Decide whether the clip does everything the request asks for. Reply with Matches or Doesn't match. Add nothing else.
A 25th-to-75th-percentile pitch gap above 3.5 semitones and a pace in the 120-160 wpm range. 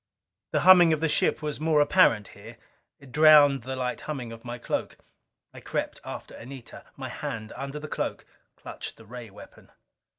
Doesn't match